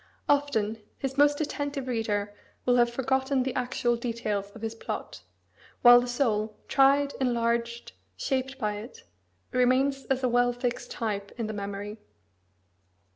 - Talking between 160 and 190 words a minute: No, average, 140 wpm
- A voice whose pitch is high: Yes, high, 245 Hz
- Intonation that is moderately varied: Yes, average, 3.2 semitones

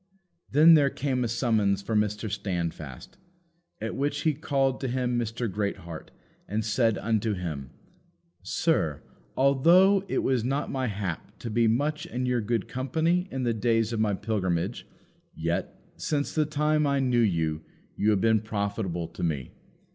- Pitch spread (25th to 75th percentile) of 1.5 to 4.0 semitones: No, average, 4.9 semitones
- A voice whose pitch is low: Yes, low, 115 Hz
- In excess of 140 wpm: Yes, average, 160 wpm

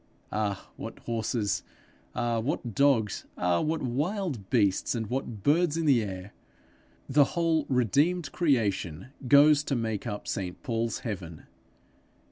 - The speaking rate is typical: No, slow, 130 wpm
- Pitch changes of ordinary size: No, wide, 5.9 semitones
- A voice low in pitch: Yes, low, 120 Hz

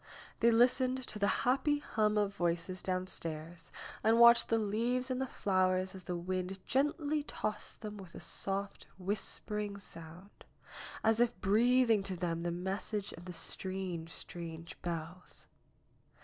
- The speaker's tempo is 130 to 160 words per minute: Yes, average, 145 wpm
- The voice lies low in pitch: No, high, 195 Hz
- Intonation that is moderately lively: Yes, average, 4.3 semitones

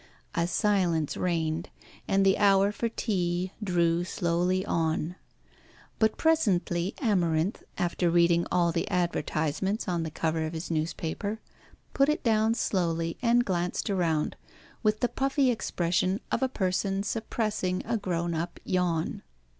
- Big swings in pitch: No, average, 3.6 semitones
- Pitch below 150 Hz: No, medium, 180 Hz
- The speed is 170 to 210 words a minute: No, slow, 135 wpm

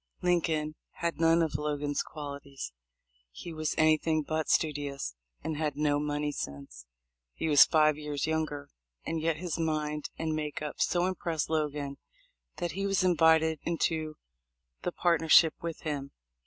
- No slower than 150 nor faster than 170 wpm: Yes, average, 155 wpm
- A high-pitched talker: No, medium, 155 Hz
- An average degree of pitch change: No, narrow, 1.7 semitones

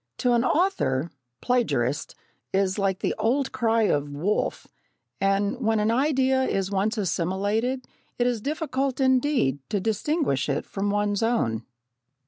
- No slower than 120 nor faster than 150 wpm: Yes, slow, 135 wpm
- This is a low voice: No, high, 220 Hz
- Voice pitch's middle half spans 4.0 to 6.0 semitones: Yes, average, 5.1 semitones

